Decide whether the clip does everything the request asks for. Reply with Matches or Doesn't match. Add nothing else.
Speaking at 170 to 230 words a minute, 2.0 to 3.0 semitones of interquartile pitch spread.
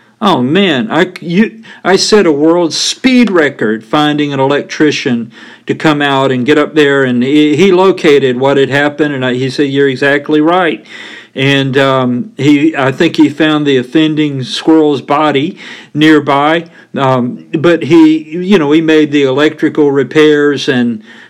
Doesn't match